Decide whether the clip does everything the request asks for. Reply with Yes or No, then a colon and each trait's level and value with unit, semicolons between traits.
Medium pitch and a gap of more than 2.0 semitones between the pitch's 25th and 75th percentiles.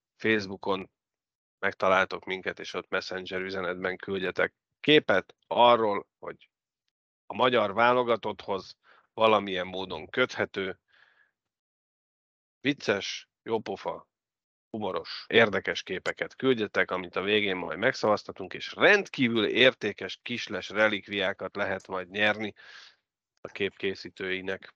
No: very low, 95 Hz; narrow, 2.6 semitones